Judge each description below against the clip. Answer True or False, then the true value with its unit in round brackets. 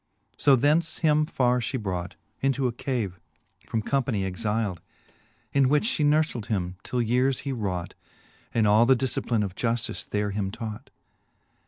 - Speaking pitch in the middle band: False (120 Hz)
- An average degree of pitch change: True (4.6 semitones)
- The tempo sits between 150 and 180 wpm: True (155 wpm)